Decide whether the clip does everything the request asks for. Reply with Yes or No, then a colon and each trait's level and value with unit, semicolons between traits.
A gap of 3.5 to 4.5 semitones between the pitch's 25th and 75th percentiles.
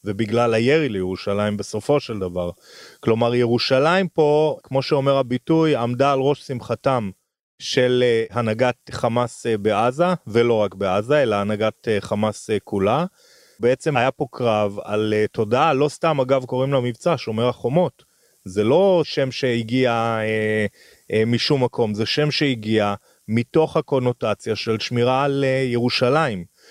Yes: average, 3.9 semitones